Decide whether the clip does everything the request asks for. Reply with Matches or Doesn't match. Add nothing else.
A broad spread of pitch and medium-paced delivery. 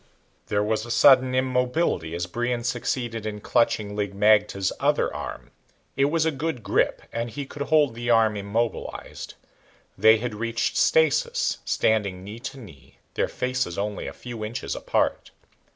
Doesn't match